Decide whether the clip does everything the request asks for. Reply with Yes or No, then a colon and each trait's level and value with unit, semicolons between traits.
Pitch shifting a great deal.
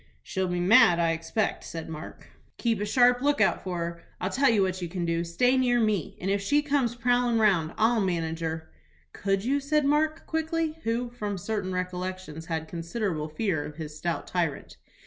Yes: wide, 6.3 semitones